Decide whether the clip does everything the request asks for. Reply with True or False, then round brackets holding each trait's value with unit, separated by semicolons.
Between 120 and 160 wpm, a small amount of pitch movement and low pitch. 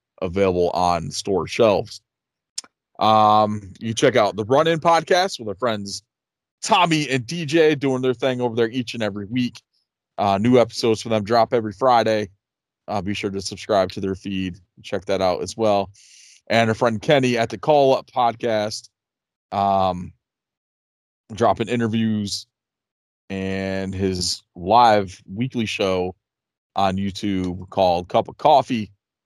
False (150 wpm; 3.9 semitones; 105 Hz)